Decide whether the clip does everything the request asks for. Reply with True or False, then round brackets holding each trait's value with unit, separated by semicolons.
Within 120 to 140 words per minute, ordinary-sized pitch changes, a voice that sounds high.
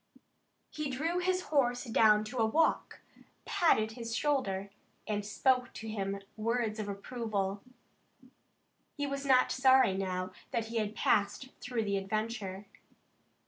True (135 wpm; 4.3 semitones; 225 Hz)